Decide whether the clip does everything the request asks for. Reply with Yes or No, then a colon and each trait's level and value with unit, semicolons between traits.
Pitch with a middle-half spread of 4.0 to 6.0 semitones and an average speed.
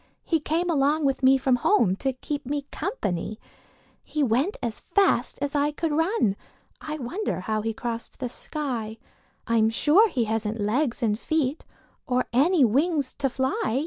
Yes: average, 5.0 semitones; average, 165 wpm